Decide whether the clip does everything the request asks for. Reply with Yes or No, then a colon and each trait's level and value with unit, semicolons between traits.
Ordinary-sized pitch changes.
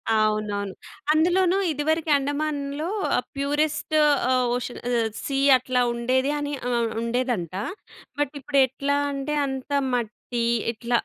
Yes: average, 3.7 semitones